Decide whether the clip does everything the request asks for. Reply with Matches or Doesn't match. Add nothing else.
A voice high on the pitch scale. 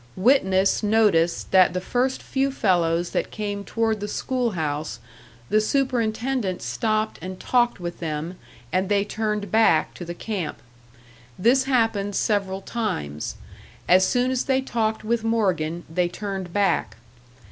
Matches